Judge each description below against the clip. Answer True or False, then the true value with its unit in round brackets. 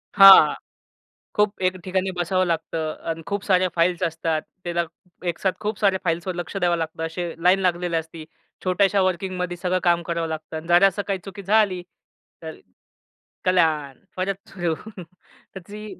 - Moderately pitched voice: True (180 Hz)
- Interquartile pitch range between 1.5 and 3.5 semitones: True (2.4 semitones)